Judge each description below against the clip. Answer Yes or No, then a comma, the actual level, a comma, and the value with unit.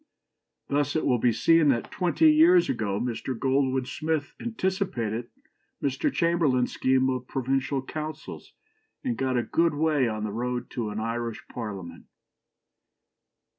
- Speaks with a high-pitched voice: No, low, 130 Hz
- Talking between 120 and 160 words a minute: Yes, average, 140 wpm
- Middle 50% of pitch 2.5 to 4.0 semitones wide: No, average, 5.0 semitones